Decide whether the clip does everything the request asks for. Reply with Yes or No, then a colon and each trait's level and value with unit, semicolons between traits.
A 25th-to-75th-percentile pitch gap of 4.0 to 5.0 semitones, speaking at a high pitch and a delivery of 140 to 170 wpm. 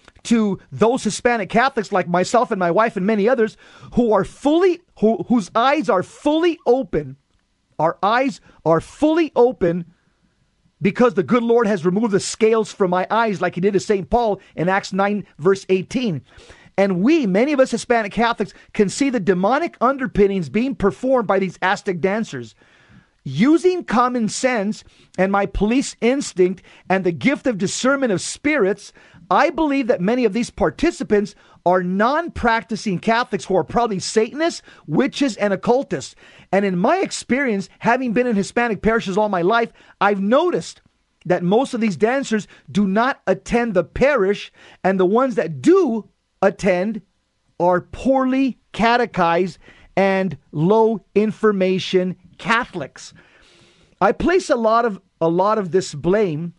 Yes: average, 4.5 semitones; high, 210 Hz; average, 155 wpm